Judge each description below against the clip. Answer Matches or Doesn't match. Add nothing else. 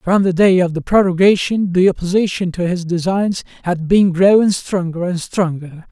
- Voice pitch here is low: Doesn't match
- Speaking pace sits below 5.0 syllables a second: Matches